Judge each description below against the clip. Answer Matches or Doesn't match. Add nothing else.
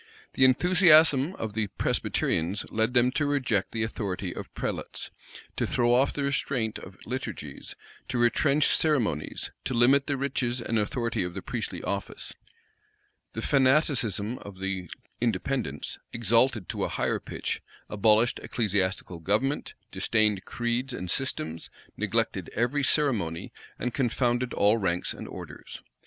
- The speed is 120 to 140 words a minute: Matches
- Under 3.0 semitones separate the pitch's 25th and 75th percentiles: Doesn't match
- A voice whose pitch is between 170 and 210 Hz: Doesn't match